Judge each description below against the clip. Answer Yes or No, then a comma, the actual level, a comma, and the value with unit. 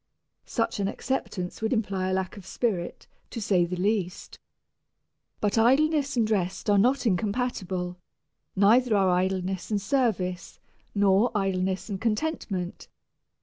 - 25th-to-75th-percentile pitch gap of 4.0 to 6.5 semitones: No, average, 3.5 semitones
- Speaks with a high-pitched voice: Yes, high, 200 Hz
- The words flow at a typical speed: No, slow, 130 wpm